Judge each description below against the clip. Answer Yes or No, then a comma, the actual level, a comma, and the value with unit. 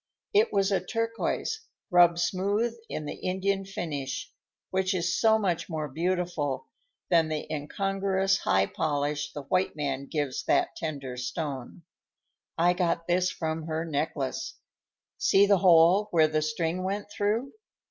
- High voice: No, medium, 170 Hz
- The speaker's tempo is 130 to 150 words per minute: Yes, average, 140 wpm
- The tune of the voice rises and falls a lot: No, average, 4.2 semitones